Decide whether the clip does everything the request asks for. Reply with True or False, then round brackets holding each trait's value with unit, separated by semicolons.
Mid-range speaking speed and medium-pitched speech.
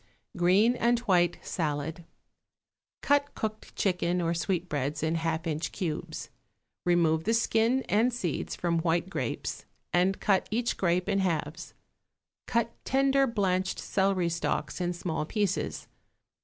False (130 wpm; 180 Hz)